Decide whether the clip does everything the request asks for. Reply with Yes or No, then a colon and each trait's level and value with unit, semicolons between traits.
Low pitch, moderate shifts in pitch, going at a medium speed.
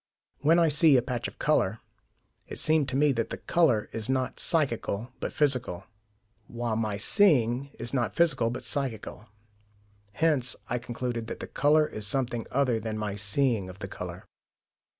Yes: low, 125 Hz; average, 4.2 semitones; average, 170 wpm